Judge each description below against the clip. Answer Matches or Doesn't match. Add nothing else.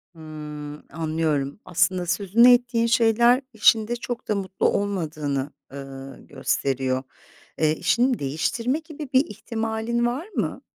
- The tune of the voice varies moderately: Doesn't match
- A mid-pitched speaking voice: Doesn't match